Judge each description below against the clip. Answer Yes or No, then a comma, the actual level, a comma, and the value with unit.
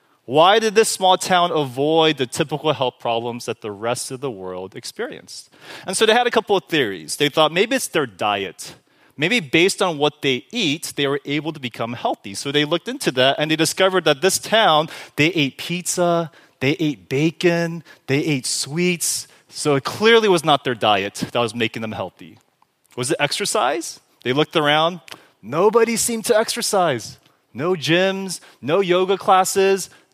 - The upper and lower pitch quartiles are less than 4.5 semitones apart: No, wide, 5.5 semitones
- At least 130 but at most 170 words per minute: No, average, 180 wpm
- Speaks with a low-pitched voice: No, medium, 155 Hz